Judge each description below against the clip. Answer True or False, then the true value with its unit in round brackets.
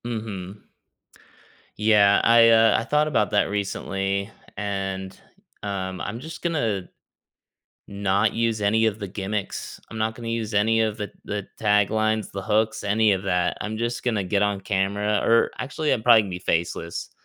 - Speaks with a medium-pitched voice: False (105 Hz)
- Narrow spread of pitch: True (2.2 semitones)